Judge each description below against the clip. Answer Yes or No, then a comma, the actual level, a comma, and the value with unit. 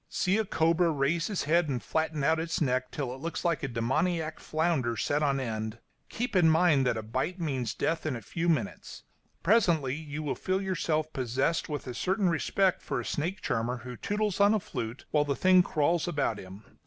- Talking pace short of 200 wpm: No, fast, 205 wpm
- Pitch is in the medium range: Yes, medium, 155 Hz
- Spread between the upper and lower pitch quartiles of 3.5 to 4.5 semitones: No, average, 4.9 semitones